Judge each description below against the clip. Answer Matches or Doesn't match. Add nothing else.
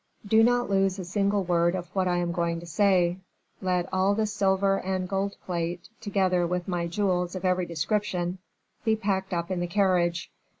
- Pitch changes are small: Matches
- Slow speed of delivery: Doesn't match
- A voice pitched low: Doesn't match